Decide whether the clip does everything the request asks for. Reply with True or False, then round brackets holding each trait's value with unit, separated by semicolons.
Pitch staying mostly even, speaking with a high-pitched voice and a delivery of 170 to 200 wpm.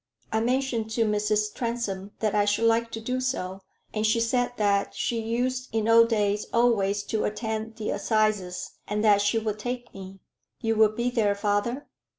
True (2.1 semitones; 220 Hz; 180 wpm)